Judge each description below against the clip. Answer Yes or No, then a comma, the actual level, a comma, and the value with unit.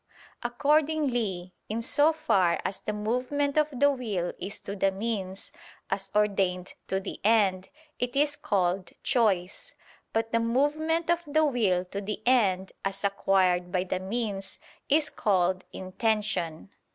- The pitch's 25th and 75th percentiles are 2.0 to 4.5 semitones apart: No, average, 5.3 semitones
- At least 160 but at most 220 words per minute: No, average, 140 wpm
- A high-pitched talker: Yes, high, 210 Hz